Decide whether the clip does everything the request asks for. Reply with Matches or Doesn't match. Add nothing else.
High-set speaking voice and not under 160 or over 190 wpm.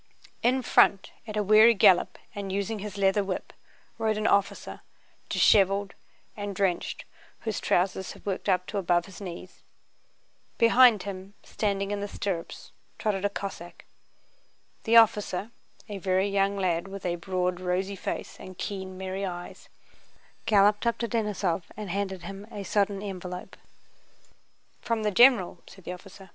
Doesn't match